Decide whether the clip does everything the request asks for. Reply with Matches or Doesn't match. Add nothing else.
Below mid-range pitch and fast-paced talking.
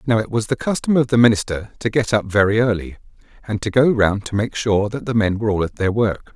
Matches